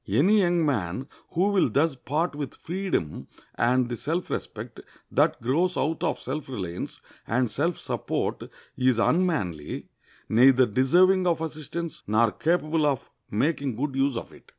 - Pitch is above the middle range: No, medium, 145 Hz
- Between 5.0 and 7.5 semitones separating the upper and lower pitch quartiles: Yes, wide, 5.4 semitones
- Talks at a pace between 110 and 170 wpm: Yes, average, 150 wpm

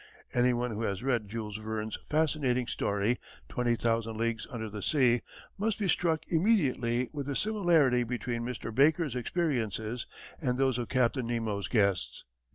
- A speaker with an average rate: Yes, average, 155 wpm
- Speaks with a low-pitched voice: Yes, low, 120 Hz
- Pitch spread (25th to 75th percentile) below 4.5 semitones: Yes, average, 3.8 semitones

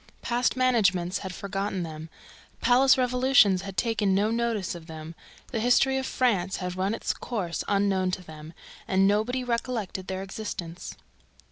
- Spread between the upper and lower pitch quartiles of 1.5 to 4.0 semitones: No, average, 4.5 semitones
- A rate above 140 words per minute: Yes, average, 150 wpm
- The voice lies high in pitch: Yes, high, 200 Hz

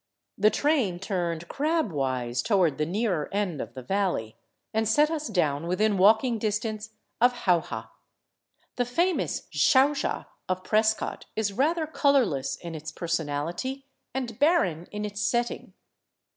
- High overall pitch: Yes, high, 205 Hz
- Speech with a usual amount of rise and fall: No, wide, 6.6 semitones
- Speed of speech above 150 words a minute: No, average, 145 wpm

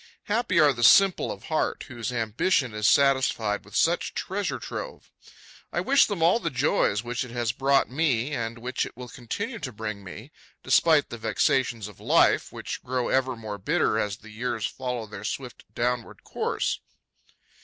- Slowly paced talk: No, average, 175 wpm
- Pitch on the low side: Yes, low, 125 Hz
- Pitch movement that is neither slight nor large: Yes, average, 4.8 semitones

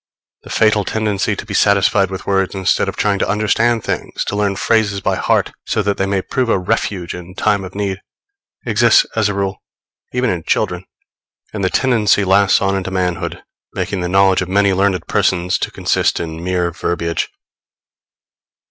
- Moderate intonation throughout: No, narrow, 1.9 semitones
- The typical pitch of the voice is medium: No, very low, 95 Hz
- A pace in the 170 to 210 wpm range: Yes, average, 180 wpm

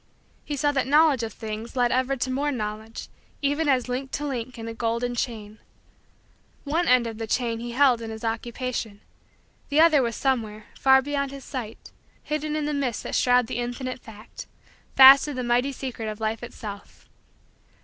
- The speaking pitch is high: Yes, very high, 250 Hz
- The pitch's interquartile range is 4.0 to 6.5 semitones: No, average, 3.4 semitones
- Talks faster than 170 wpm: Yes, average, 185 wpm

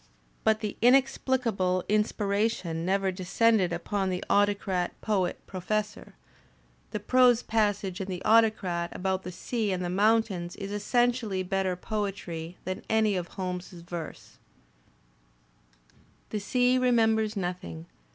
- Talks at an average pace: No, slow, 120 wpm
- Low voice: No, high, 200 Hz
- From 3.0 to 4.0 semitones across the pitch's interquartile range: Yes, average, 3.3 semitones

